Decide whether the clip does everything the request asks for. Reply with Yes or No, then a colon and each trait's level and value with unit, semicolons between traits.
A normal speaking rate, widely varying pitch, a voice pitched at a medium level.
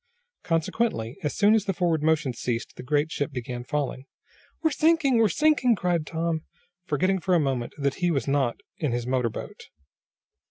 Yes: average, 175 wpm; wide, 6.3 semitones; medium, 155 Hz